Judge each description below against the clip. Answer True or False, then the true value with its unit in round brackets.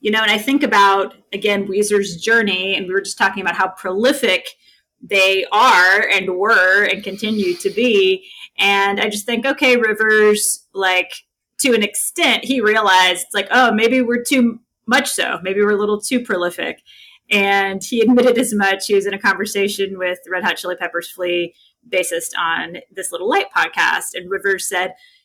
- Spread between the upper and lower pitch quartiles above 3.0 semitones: True (3.7 semitones)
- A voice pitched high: True (205 Hz)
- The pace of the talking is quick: False (180 wpm)